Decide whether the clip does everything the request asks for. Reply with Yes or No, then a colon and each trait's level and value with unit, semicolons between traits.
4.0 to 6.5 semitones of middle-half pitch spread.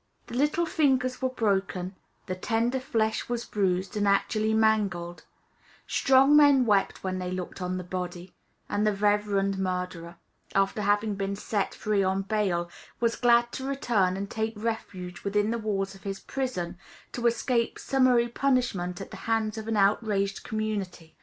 No: average, 3.6 semitones